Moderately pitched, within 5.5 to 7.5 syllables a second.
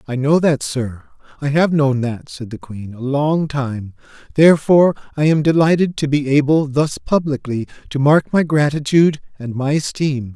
No: medium, 145 Hz; 4.8 syllables/s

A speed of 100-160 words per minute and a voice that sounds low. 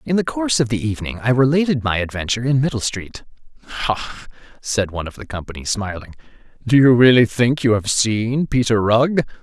No: average, 185 wpm; low, 120 Hz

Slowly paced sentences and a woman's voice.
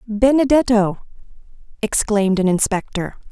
Yes: slow, 70 wpm; female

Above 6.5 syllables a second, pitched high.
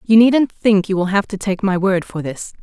No: 4.9 syllables/s; high, 195 Hz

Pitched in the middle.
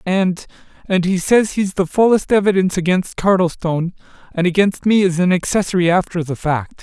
Yes: medium, 180 Hz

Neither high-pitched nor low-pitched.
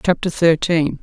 Yes: medium, 165 Hz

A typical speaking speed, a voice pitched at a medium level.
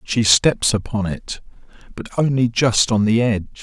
No: average, 165 wpm; low, 110 Hz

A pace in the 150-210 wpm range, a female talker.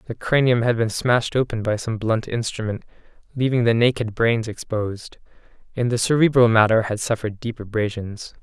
No: average, 165 wpm; male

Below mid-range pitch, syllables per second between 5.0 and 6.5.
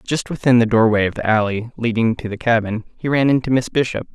Yes: low, 115 Hz; 6.0 syllables/s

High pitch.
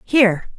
Yes: high, 220 Hz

